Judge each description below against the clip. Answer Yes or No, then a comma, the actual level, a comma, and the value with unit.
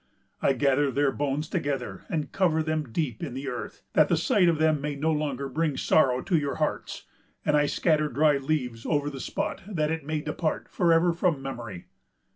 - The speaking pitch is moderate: Yes, medium, 150 Hz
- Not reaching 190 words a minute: No, average, 200 wpm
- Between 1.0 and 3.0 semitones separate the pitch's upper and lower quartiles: Yes, narrow, 2.6 semitones